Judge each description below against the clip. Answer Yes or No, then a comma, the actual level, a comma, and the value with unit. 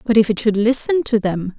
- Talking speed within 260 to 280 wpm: Yes, fast, 265 wpm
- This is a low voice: No, high, 225 Hz